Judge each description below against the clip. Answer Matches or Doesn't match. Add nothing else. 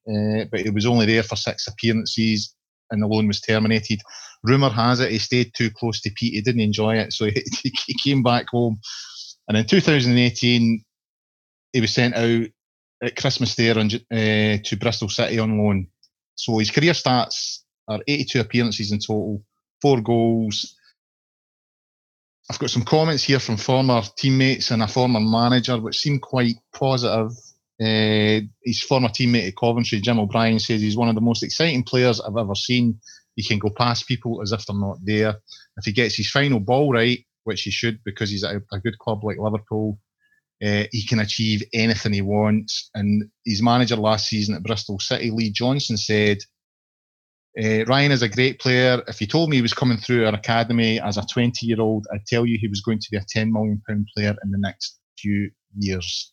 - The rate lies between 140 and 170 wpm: Doesn't match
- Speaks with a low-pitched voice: Matches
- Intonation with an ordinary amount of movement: Doesn't match